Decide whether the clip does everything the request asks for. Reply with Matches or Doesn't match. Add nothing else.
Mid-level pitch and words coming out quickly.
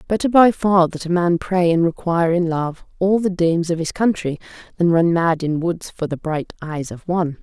Matches